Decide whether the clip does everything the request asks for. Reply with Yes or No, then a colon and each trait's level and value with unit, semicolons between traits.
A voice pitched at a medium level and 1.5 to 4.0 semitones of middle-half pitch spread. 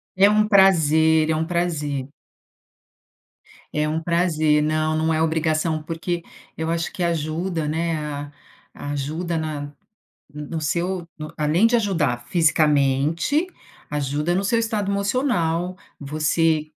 Yes: medium, 160 Hz; narrow, 2.5 semitones